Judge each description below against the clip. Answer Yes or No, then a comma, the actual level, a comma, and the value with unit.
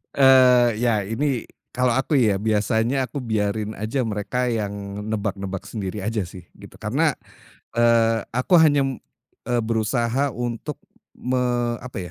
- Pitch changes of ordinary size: Yes, average, 3.0 semitones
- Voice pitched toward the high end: No, low, 115 Hz